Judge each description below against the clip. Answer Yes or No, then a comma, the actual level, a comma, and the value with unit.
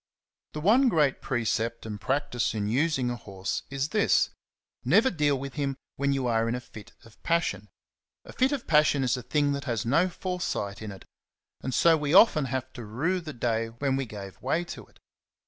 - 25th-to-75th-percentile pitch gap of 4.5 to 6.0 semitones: Yes, average, 5.1 semitones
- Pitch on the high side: No, low, 135 Hz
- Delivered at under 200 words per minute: No, fast, 205 wpm